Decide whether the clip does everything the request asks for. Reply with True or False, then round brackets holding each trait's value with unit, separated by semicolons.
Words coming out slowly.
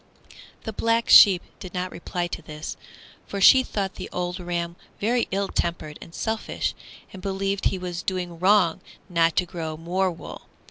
False (165 wpm)